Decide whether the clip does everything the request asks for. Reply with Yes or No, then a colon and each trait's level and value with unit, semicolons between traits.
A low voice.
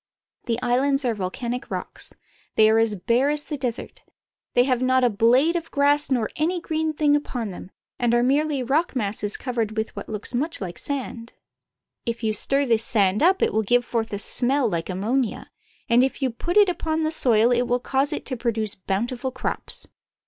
No: high, 245 Hz